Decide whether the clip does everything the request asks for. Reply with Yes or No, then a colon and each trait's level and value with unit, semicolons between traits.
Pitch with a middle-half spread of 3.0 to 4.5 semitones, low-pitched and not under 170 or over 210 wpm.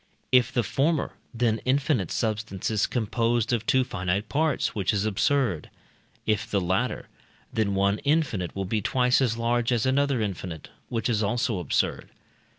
No: average, 4.1 semitones; low, 115 Hz; average, 155 wpm